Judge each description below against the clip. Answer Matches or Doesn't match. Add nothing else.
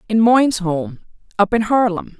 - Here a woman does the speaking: Matches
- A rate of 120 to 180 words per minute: Matches